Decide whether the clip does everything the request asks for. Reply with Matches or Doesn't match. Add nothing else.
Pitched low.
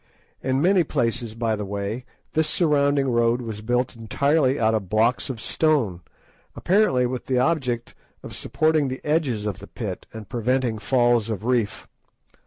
Matches